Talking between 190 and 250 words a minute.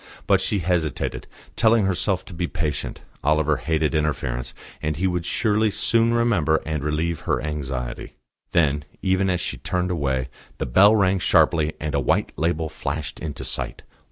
No: average, 160 wpm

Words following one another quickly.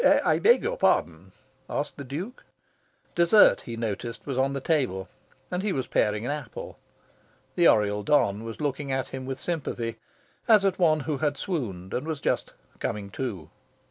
No: average, 175 wpm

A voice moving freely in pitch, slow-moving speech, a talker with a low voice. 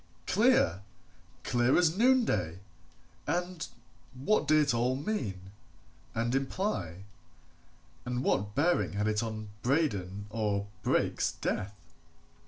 Yes: wide, 7.9 semitones; slow, 105 wpm; low, 120 Hz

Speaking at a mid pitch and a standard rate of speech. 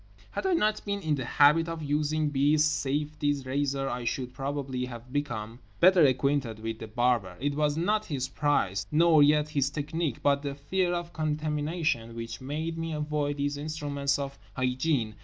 Yes: medium, 145 Hz; average, 175 wpm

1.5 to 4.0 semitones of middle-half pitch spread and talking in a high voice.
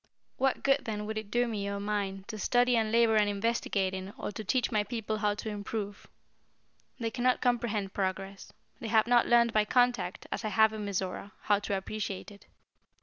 Yes: narrow, 2.6 semitones; high, 215 Hz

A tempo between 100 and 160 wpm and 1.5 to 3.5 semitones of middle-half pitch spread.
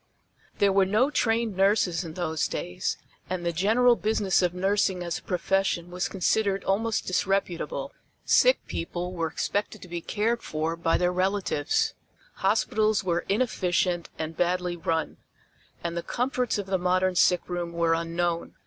Yes: average, 150 wpm; average, 3.0 semitones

